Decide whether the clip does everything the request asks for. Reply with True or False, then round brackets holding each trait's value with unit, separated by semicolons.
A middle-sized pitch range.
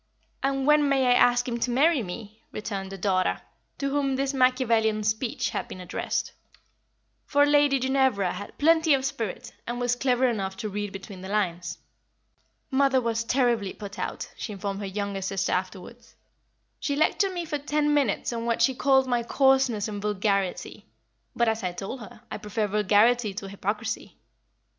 True (4.8 semitones)